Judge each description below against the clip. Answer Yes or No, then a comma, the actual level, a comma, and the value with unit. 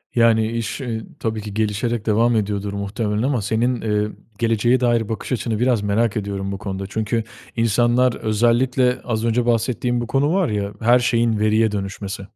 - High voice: No, low, 115 Hz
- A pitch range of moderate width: No, narrow, 2.2 semitones